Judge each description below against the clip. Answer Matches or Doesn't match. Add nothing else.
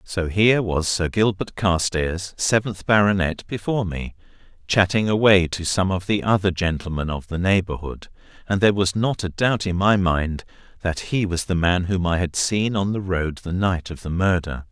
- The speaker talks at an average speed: Matches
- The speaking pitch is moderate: Doesn't match